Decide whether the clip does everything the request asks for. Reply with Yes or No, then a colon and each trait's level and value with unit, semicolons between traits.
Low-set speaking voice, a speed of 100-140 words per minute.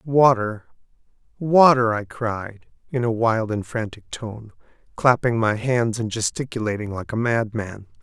Yes: low, 115 Hz; slow, 135 wpm